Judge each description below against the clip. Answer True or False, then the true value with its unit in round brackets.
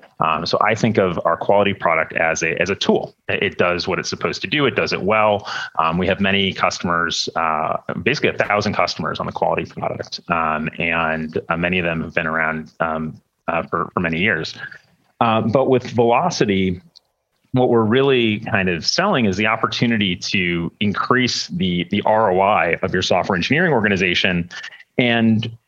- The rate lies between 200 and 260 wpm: False (180 wpm)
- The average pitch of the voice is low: True (100 Hz)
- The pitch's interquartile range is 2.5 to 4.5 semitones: False (5.0 semitones)